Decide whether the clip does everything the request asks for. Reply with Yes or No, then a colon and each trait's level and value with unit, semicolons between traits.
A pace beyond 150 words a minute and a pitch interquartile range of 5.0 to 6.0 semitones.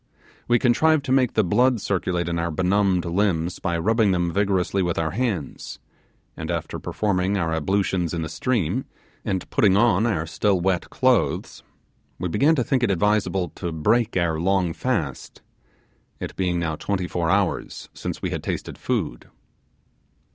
No: average, 160 wpm; average, 4.0 semitones